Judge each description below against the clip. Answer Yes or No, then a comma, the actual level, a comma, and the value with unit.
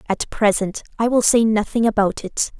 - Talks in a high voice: Yes, high, 215 Hz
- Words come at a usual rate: Yes, average, 185 wpm